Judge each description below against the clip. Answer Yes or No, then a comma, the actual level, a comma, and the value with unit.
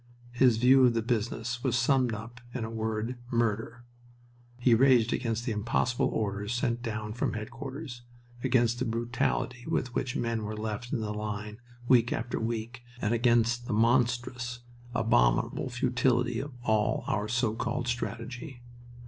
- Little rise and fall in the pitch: Yes, narrow, 1.8 semitones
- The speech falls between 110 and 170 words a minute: Yes, average, 150 wpm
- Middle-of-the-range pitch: No, low, 120 Hz